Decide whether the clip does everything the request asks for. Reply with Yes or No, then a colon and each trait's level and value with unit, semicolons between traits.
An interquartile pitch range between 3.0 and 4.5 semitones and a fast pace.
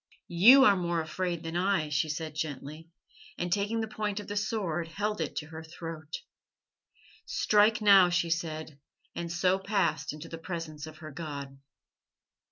No: average, 4.1 semitones; average, 165 wpm